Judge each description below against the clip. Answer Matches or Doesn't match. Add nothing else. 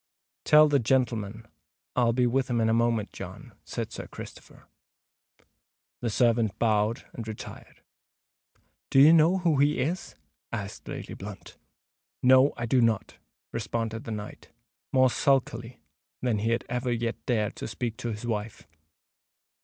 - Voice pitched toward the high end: Doesn't match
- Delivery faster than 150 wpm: Doesn't match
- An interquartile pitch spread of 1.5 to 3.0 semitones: Matches